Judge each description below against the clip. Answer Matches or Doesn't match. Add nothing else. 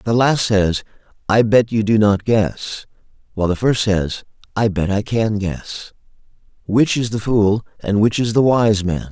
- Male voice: Matches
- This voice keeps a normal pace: Matches